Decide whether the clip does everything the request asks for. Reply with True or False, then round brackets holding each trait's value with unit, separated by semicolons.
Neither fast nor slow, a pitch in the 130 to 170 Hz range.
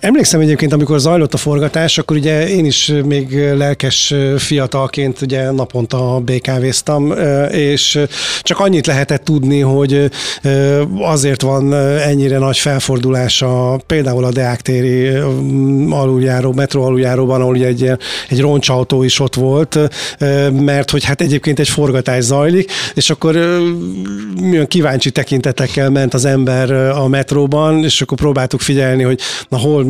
True (135 wpm; 140 Hz)